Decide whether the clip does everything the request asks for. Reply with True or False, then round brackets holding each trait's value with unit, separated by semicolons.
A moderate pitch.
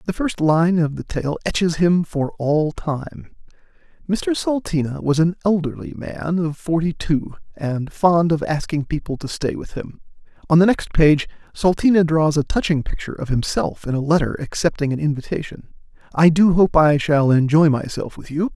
True (160 Hz)